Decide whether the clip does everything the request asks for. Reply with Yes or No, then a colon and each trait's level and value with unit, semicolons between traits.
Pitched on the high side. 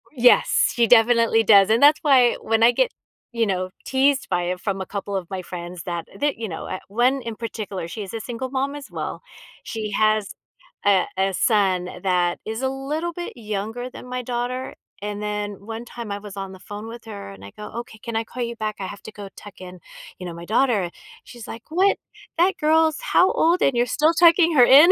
Yes: high, 225 Hz